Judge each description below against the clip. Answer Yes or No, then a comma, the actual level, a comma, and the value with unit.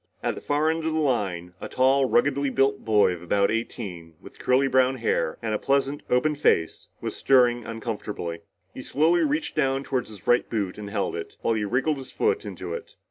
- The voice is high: No, low, 125 Hz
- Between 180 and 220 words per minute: Yes, fast, 205 wpm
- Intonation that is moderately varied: Yes, average, 5.0 semitones